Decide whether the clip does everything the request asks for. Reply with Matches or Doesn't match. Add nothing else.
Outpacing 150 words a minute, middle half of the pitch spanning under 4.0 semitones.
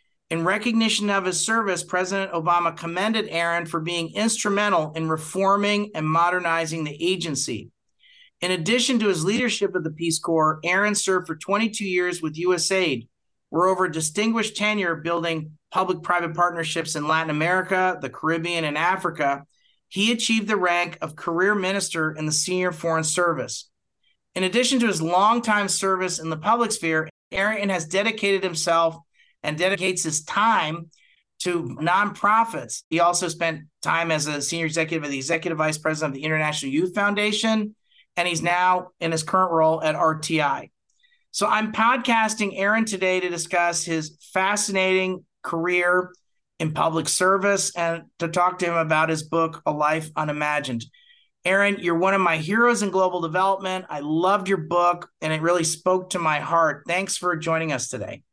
Matches